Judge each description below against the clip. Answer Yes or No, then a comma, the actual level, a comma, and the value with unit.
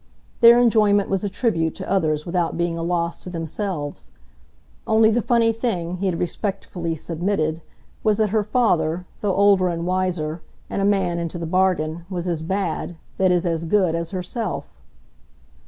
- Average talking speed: Yes, average, 170 wpm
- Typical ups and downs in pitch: Yes, average, 3.3 semitones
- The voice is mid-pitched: Yes, medium, 180 Hz